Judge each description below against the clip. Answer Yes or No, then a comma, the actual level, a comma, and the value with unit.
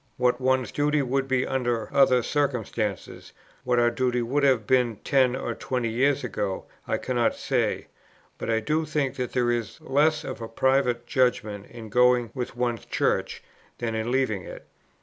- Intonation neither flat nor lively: No, narrow, 2.2 semitones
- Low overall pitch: Yes, low, 125 Hz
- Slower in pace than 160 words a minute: No, average, 170 wpm